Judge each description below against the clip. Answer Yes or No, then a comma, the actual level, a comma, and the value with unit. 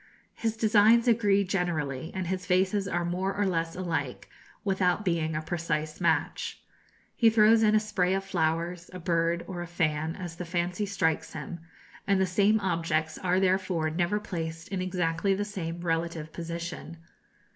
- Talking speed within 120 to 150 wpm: No, average, 165 wpm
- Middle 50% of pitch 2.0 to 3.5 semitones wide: Yes, average, 2.9 semitones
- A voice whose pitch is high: No, medium, 180 Hz